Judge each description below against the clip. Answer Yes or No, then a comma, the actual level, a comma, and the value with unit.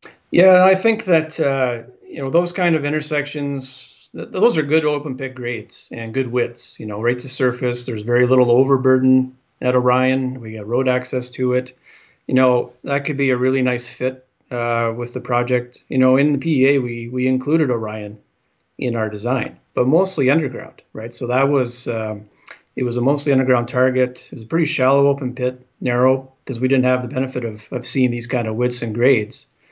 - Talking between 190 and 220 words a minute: Yes, average, 200 wpm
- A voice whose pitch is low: Yes, low, 130 Hz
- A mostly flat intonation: Yes, narrow, 1.7 semitones